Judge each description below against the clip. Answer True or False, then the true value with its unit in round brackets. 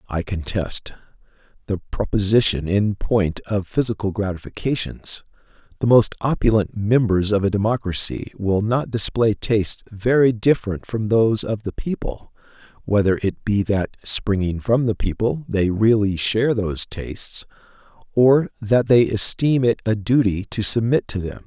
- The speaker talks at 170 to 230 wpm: False (145 wpm)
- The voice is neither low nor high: False (105 Hz)